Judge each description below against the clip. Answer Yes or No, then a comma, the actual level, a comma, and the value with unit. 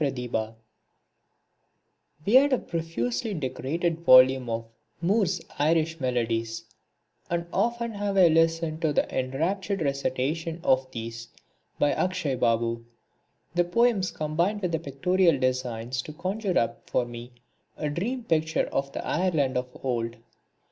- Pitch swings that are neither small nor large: No, wide, 6.0 semitones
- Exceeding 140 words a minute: No, slow, 135 wpm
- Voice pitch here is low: No, medium, 155 Hz